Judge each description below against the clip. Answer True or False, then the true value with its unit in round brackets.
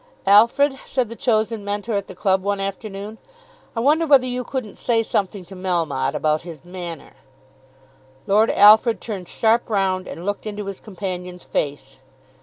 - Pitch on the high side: True (200 Hz)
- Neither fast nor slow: True (160 wpm)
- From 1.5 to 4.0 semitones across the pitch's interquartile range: True (3.7 semitones)